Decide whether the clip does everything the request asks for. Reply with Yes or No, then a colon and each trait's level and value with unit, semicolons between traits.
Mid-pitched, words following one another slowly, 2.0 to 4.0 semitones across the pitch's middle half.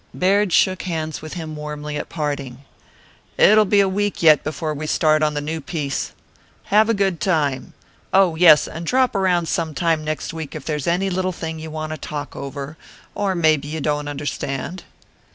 No: medium, 160 Hz; average, 190 wpm; average, 3.6 semitones